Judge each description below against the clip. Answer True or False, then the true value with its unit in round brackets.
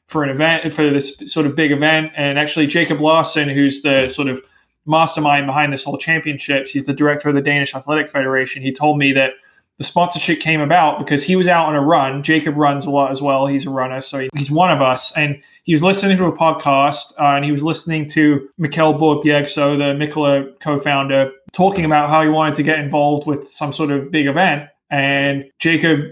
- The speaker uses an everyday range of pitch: False (2.0 semitones)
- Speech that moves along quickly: True (215 wpm)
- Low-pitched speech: False (145 Hz)